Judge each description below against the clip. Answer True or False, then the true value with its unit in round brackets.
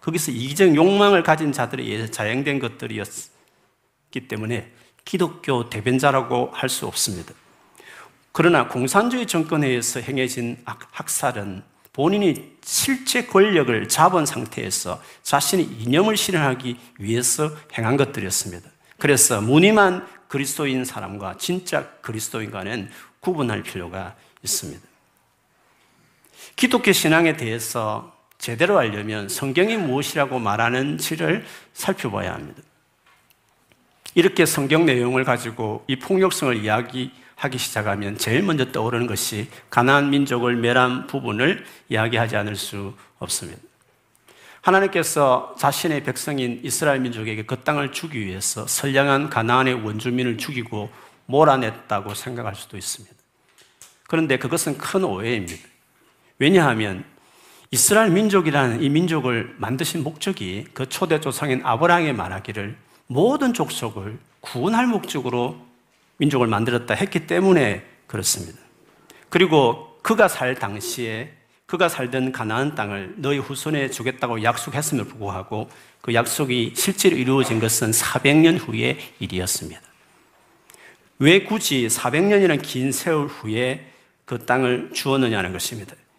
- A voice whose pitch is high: False (130 Hz)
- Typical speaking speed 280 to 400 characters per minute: True (305 characters per minute)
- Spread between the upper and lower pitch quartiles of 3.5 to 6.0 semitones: True (5.2 semitones)